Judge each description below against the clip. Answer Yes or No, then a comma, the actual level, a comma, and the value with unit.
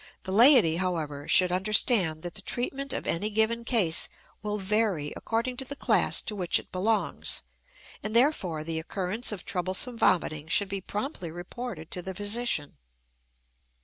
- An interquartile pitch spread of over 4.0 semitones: Yes, average, 4.8 semitones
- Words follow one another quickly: No, average, 155 wpm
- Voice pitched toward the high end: Yes, high, 195 Hz